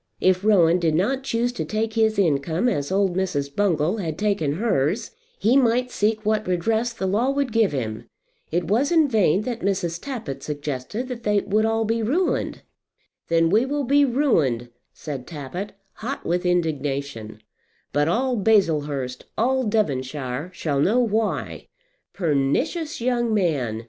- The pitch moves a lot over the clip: Yes, wide, 7.3 semitones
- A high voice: Yes, high, 200 Hz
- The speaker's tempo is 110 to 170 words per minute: Yes, average, 155 wpm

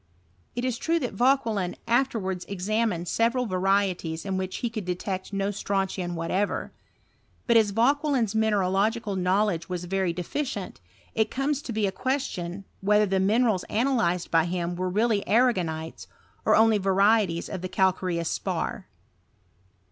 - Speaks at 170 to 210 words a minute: No, average, 145 wpm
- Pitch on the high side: Yes, high, 200 Hz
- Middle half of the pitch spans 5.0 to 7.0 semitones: No, average, 3.9 semitones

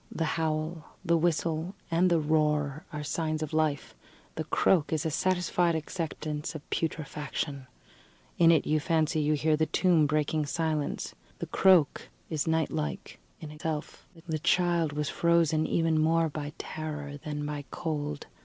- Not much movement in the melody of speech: Yes, narrow, 1.6 semitones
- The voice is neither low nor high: Yes, medium, 155 Hz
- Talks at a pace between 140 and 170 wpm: Yes, average, 155 wpm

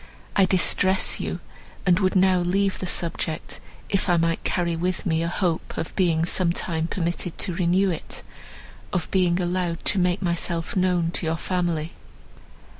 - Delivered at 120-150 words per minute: No, average, 165 wpm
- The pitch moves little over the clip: Yes, narrow, 1.7 semitones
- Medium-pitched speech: Yes, medium, 175 Hz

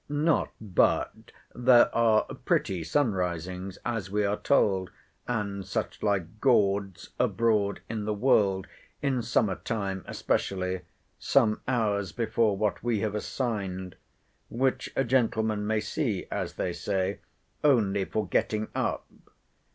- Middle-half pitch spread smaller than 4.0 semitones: Yes, average, 3.2 semitones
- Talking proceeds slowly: Yes, slow, 130 wpm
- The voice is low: Yes, low, 105 Hz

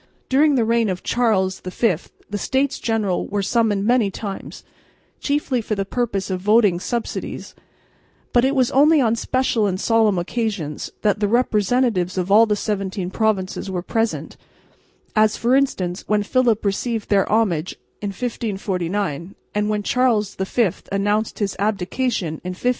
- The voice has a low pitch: No, high, 210 Hz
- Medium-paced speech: Yes, average, 155 wpm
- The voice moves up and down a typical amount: Yes, average, 3.5 semitones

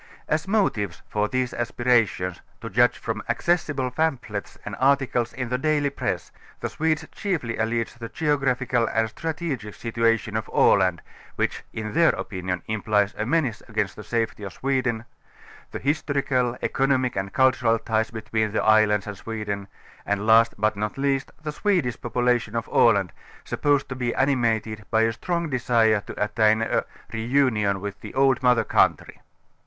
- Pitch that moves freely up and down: No, average, 3.7 semitones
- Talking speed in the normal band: Yes, average, 160 wpm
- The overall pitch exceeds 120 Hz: No, low, 115 Hz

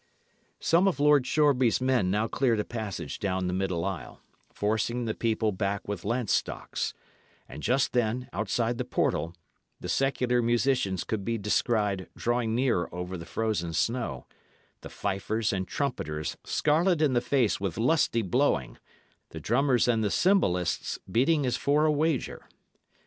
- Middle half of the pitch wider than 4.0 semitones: Yes, average, 5.0 semitones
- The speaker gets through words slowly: No, average, 155 wpm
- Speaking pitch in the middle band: No, low, 115 Hz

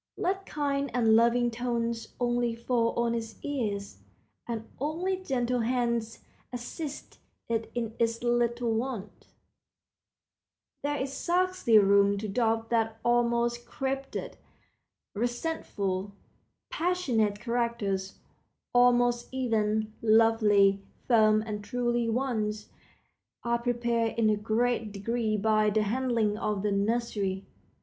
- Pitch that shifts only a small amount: Yes, narrow, 2.2 semitones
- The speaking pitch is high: Yes, high, 235 Hz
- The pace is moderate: No, slow, 110 wpm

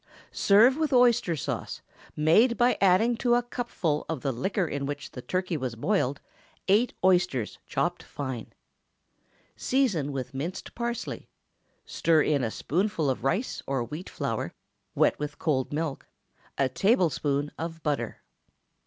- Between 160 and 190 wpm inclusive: No, average, 140 wpm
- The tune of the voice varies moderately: No, wide, 7.4 semitones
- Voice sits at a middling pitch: Yes, medium, 165 Hz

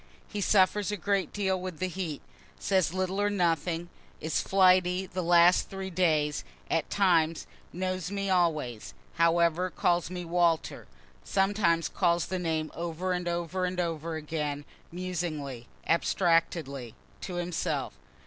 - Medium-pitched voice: Yes, medium, 175 Hz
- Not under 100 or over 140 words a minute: Yes, slow, 135 wpm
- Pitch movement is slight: Yes, narrow, 2.2 semitones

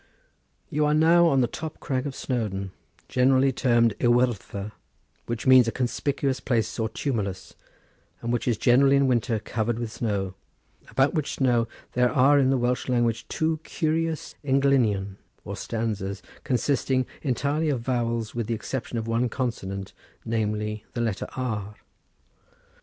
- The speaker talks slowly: No, average, 150 wpm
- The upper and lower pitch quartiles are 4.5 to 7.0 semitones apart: No, average, 3.3 semitones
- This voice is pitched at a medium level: No, low, 120 Hz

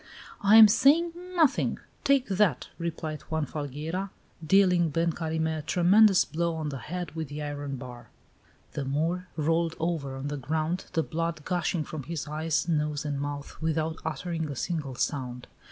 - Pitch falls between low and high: Yes, medium, 160 Hz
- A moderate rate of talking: Yes, average, 165 wpm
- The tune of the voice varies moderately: Yes, average, 3.0 semitones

